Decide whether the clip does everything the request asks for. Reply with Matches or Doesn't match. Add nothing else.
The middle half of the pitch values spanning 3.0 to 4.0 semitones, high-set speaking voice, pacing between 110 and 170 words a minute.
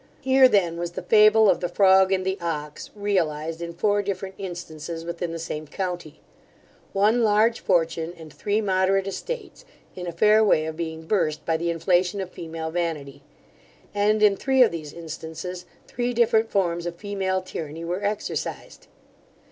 Doesn't match